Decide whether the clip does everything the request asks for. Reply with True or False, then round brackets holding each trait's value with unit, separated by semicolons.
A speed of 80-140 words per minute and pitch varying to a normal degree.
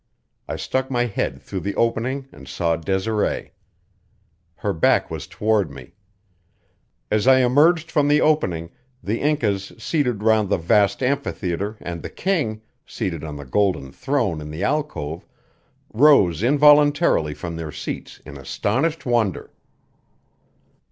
False (135 wpm; 8.1 semitones)